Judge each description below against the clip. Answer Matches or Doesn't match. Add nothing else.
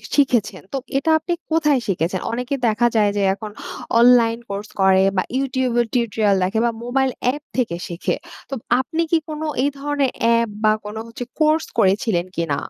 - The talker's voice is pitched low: Doesn't match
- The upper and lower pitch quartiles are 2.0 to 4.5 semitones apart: Doesn't match